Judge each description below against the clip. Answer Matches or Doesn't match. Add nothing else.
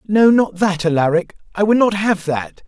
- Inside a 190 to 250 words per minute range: Matches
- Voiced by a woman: Doesn't match